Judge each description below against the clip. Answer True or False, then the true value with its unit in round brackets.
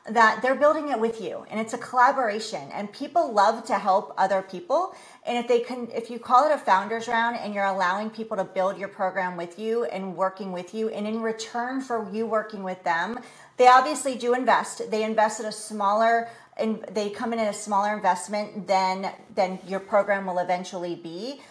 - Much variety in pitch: False (3.7 semitones)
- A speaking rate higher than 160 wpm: True (205 wpm)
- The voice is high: True (215 Hz)